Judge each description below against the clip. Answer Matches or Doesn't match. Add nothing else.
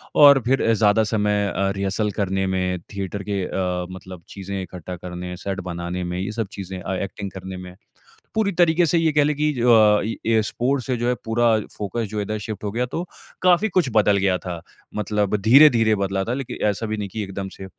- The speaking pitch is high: Doesn't match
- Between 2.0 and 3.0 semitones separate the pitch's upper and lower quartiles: Doesn't match